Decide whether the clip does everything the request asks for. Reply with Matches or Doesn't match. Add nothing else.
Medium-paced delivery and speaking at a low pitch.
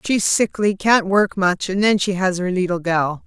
Doesn't match